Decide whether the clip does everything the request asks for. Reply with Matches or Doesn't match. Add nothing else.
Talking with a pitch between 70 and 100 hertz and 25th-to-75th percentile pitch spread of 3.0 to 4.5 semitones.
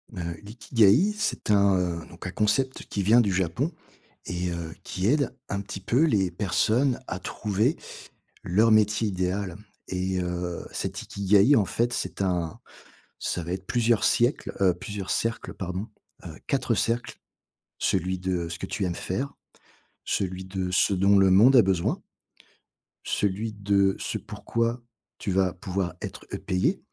Matches